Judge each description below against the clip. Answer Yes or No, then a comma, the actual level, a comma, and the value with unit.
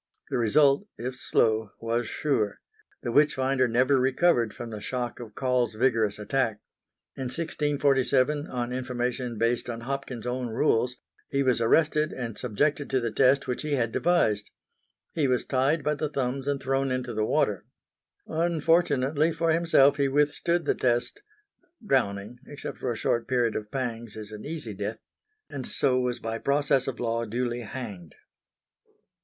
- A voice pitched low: Yes, low, 130 Hz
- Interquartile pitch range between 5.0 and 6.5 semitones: No, average, 3.4 semitones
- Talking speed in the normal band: Yes, average, 160 wpm